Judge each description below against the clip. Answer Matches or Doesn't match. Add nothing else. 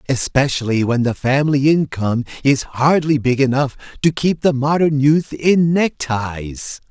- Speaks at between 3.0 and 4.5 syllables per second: Matches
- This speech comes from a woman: Doesn't match